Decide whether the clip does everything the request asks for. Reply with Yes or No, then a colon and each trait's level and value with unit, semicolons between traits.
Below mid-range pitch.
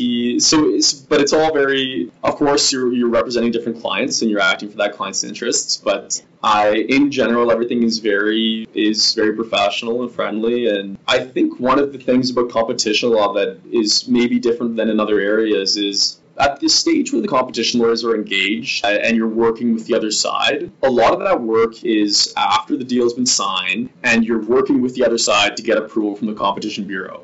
Yes: low, 115 Hz